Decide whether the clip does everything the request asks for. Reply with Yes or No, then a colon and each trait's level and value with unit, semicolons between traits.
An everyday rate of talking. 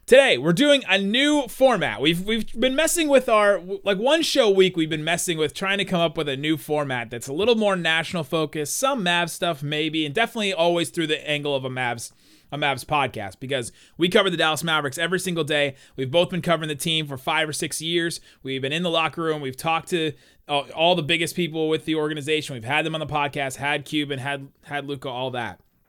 No: fast, 230 wpm